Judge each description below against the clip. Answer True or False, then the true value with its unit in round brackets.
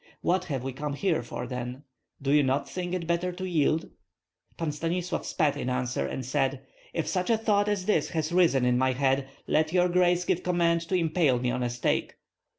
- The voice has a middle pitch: True (155 Hz)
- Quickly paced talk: True (210 wpm)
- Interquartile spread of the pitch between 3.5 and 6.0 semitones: True (5.2 semitones)